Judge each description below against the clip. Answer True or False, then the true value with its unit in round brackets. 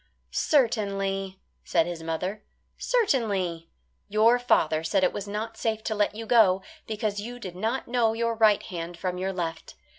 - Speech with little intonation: False (3.7 semitones)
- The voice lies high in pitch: True (205 Hz)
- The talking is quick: False (160 wpm)